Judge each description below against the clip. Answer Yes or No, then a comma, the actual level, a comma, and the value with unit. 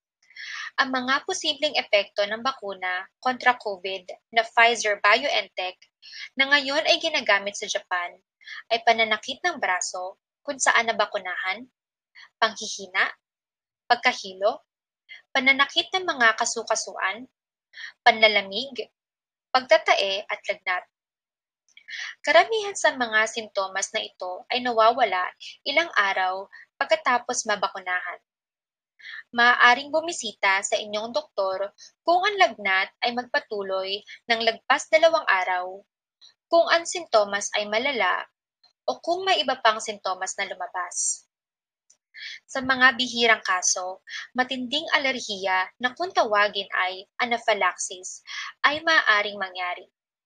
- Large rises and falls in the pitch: Yes, wide, 6.5 semitones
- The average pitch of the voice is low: No, high, 230 Hz